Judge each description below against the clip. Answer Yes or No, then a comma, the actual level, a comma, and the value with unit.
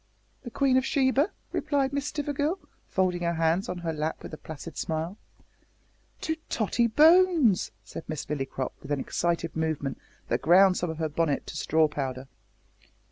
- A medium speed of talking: Yes, average, 165 wpm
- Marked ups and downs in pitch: Yes, wide, 9.0 semitones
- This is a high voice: No, medium, 175 Hz